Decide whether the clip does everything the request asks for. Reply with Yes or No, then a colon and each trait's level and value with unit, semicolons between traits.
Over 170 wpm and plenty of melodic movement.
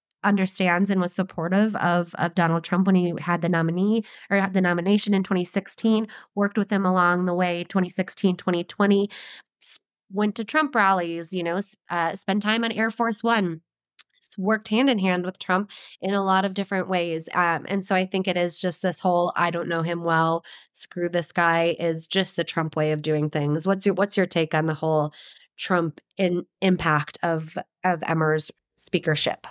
No: average, 190 wpm; average, 2.8 semitones